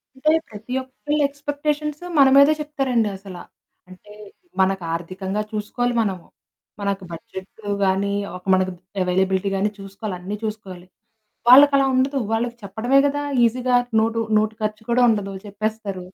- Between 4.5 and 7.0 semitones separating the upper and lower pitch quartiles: Yes, average, 5.0 semitones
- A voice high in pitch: Yes, high, 215 Hz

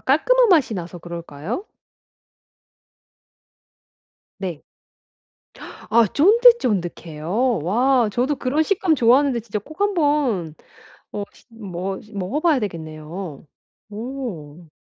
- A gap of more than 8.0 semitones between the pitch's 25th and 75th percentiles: Yes, wide, 8.7 semitones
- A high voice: Yes, high, 225 Hz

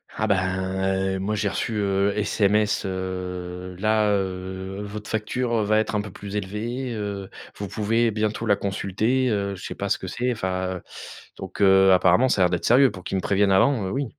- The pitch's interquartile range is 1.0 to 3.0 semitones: Yes, narrow, 2.4 semitones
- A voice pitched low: Yes, low, 100 Hz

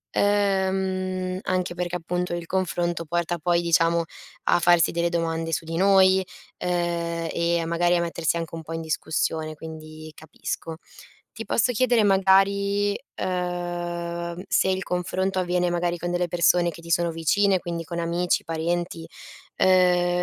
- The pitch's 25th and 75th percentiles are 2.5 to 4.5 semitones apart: No, narrow, 1.8 semitones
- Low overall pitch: No, medium, 175 Hz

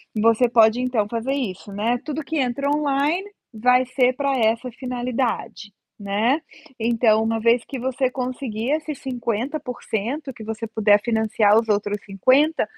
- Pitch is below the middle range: No, high, 240 Hz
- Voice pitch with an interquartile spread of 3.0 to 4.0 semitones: Yes, average, 3.3 semitones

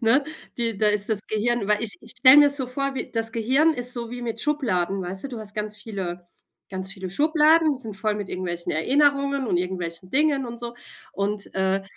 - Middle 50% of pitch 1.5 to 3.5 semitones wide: No, wide, 5.5 semitones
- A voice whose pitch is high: Yes, high, 225 Hz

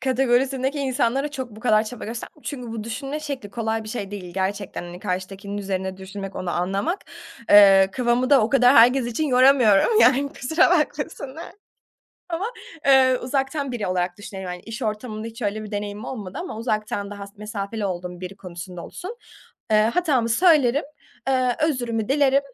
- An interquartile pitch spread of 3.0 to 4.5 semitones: No, average, 5.1 semitones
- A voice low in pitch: No, high, 230 Hz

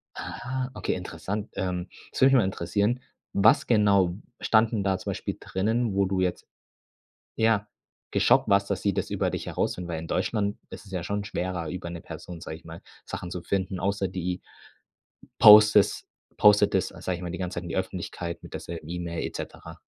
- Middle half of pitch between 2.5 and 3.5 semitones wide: Yes, average, 2.8 semitones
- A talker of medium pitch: No, very low, 95 Hz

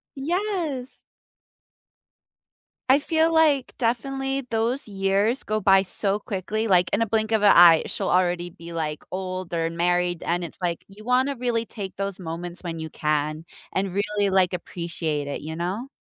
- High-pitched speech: Yes, high, 195 Hz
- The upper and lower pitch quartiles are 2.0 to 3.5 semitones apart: No, average, 5.2 semitones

